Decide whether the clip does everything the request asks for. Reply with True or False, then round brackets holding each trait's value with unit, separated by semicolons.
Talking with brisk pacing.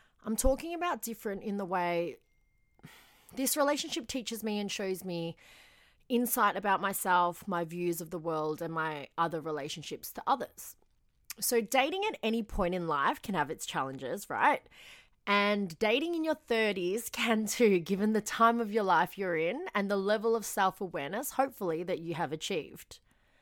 False (170 wpm)